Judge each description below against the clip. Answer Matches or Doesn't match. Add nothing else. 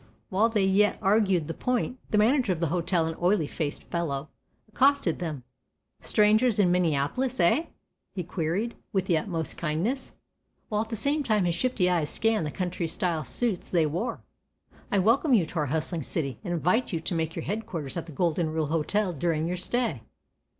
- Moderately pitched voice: Matches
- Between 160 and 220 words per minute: Matches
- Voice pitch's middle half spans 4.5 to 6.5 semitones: Matches